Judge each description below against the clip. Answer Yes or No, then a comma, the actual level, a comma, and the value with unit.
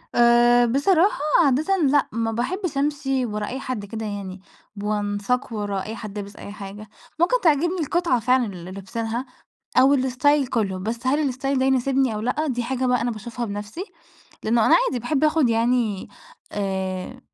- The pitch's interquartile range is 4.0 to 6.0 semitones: Yes, average, 4.5 semitones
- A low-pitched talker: No, high, 240 Hz